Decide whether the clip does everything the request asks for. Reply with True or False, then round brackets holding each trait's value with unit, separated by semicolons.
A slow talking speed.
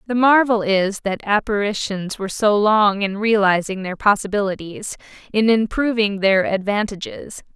True (125 wpm)